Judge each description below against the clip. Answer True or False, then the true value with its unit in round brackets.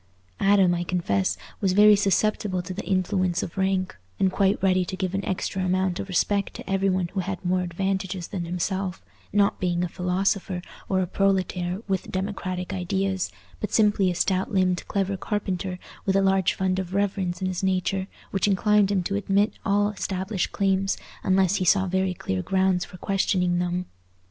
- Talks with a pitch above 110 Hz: True (190 Hz)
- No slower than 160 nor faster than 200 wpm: True (180 wpm)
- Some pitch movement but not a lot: False (1.3 semitones)